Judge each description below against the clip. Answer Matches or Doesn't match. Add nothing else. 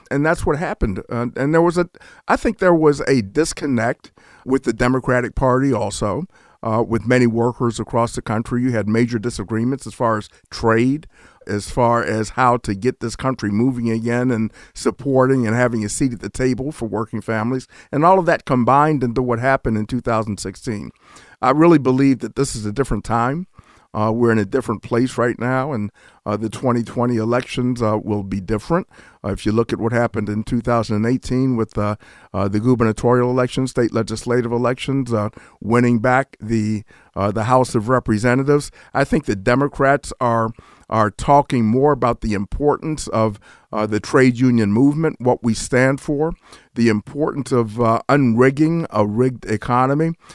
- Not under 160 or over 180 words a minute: Matches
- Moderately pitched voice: Doesn't match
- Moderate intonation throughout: Matches